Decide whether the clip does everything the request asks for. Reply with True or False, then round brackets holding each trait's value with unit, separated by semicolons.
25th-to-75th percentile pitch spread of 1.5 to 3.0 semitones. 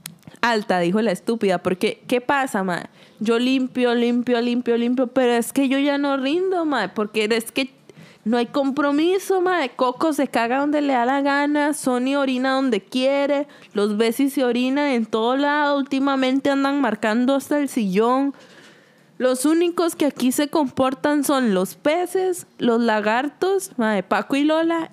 False (3.7 semitones)